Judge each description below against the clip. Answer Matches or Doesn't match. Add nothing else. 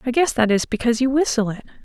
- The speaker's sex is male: Doesn't match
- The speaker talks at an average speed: Doesn't match